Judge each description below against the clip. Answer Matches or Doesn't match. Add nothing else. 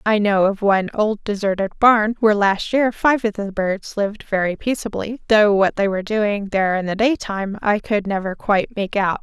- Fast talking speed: Matches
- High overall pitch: Matches